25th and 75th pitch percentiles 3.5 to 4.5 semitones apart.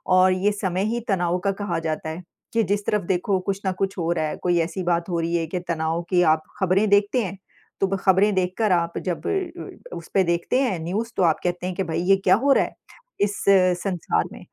No: narrow, 2.5 semitones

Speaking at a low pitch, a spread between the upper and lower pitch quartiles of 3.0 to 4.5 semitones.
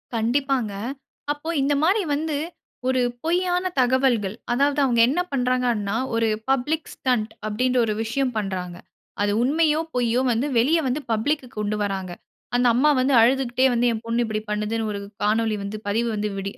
No: high, 245 Hz; average, 4.1 semitones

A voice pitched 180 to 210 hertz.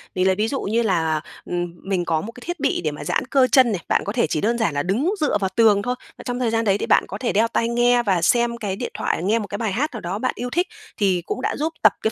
No: high, 220 Hz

